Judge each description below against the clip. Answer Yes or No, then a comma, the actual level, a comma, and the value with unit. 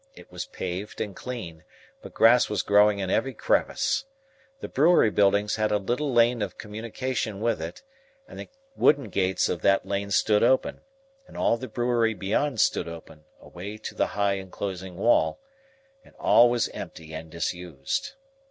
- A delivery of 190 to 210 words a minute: No, average, 165 wpm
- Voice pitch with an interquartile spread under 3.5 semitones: No, average, 4.2 semitones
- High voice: No, low, 105 Hz